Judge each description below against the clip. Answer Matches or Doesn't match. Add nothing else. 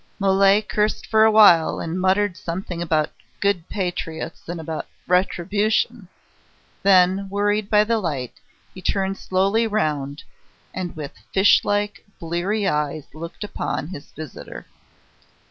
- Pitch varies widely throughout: Doesn't match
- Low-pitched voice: Doesn't match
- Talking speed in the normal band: Doesn't match